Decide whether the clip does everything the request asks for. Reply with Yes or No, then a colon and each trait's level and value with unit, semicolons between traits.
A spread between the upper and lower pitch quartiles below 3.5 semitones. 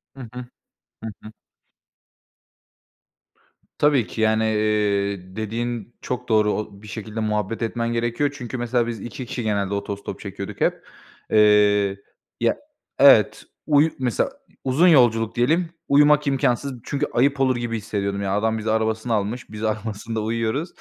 Yes: average, 2.8 semitones